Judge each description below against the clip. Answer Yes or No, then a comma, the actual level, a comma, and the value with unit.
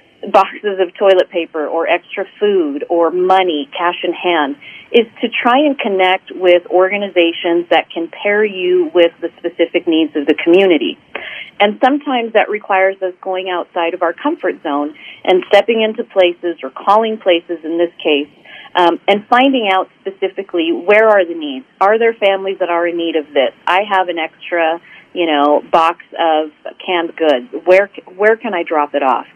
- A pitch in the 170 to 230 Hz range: Yes, medium, 185 Hz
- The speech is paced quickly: No, average, 175 wpm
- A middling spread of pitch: Yes, average, 3.6 semitones